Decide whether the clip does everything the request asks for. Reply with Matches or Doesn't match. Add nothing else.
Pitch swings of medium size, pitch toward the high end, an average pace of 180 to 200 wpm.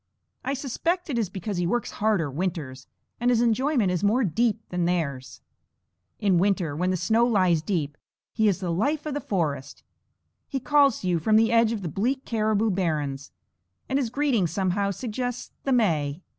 Doesn't match